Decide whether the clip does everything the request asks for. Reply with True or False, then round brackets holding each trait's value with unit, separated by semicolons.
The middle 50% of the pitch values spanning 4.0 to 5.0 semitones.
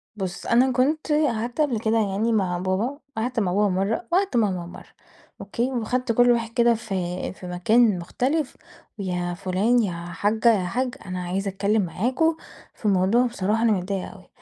True (4.5 semitones)